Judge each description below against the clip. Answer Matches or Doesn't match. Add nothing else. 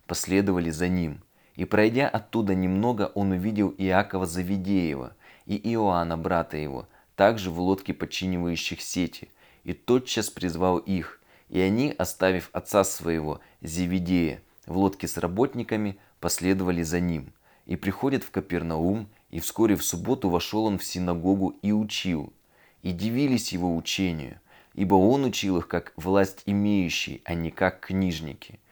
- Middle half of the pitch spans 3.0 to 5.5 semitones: Doesn't match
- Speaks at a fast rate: Doesn't match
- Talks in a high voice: Doesn't match